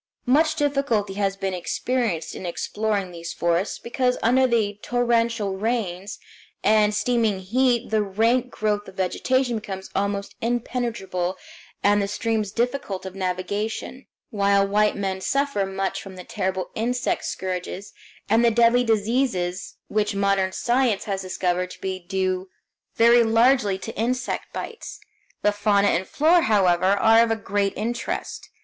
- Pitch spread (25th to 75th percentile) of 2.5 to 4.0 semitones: Yes, average, 3.6 semitones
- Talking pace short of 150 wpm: Yes, average, 140 wpm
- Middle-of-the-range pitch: No, high, 210 Hz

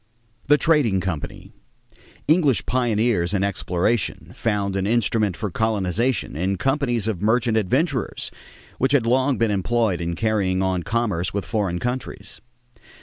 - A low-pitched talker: Yes, low, 110 Hz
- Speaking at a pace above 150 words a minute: No, slow, 135 wpm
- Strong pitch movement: No, average, 4.2 semitones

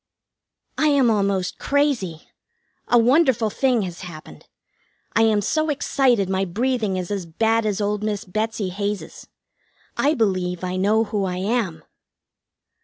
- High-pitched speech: Yes, high, 210 Hz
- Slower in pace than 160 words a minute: Yes, average, 140 wpm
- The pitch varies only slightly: No, average, 4.1 semitones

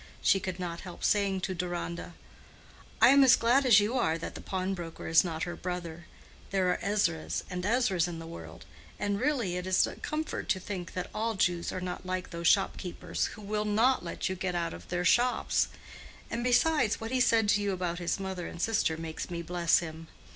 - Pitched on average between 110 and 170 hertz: No, medium, 185 Hz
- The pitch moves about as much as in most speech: Yes, average, 3.5 semitones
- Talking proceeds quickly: Yes, fast, 210 wpm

